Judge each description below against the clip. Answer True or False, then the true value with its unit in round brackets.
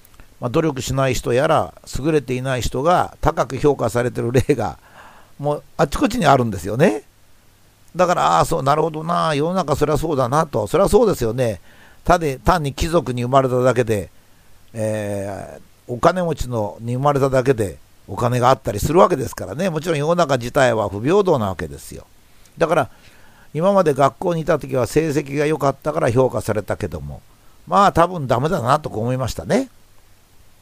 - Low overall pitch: True (130 Hz)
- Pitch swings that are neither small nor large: False (6.1 semitones)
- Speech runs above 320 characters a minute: True (355 characters per minute)